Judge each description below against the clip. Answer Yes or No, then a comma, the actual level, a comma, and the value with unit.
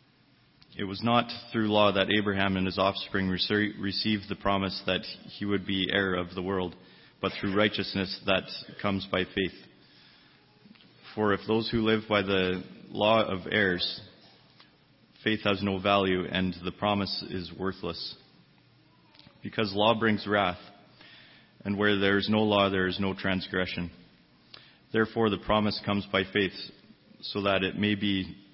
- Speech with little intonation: Yes, narrow, 1.8 semitones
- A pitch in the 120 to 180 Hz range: No, low, 100 Hz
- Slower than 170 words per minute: Yes, average, 150 wpm